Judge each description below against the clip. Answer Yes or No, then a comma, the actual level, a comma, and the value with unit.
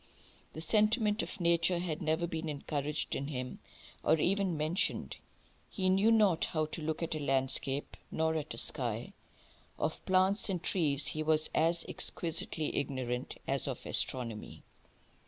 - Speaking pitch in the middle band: Yes, medium, 160 Hz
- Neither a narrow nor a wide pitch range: Yes, average, 3.8 semitones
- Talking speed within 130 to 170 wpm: Yes, average, 150 wpm